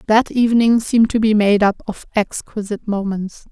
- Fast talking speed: No, average, 170 wpm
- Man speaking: No, female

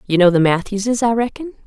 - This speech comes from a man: No, female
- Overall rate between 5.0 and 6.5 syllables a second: Yes, 5.7 syllables/s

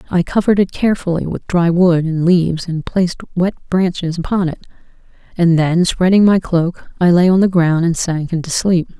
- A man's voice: No, female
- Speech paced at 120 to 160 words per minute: No, average, 195 wpm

